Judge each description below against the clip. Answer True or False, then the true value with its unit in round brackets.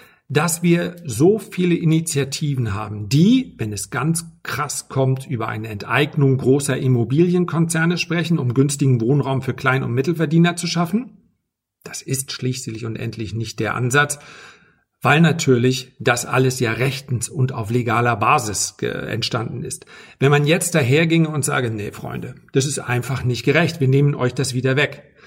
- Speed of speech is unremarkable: True (160 wpm)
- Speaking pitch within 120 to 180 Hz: True (135 Hz)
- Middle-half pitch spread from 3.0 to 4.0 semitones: False (4.5 semitones)